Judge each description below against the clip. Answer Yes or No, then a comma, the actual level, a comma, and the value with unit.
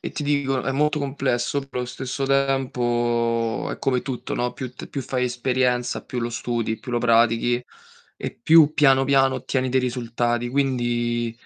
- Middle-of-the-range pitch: No, low, 125 Hz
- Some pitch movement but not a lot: No, narrow, 2.2 semitones